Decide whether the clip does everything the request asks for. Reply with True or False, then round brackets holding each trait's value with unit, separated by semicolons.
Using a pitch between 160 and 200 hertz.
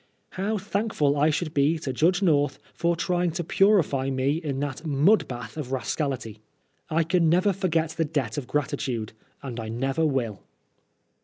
False (150 Hz)